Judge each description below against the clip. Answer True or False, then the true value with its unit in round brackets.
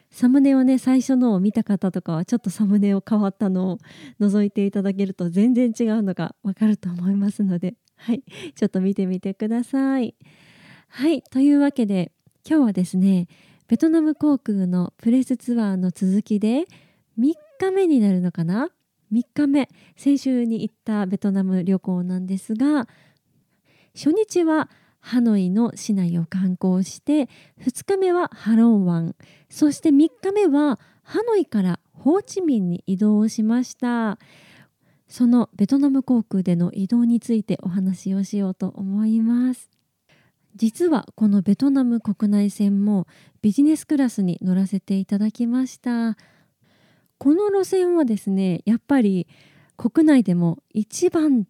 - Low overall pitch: False (215 Hz)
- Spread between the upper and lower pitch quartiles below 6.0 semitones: True (5.5 semitones)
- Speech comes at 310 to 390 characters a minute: False (290 characters per minute)